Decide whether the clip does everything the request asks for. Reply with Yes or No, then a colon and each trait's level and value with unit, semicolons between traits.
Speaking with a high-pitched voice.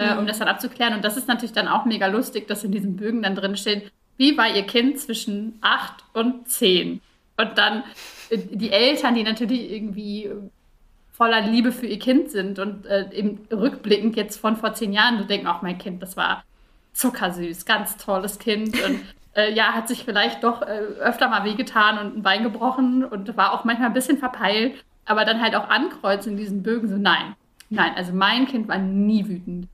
Yes: high, 215 Hz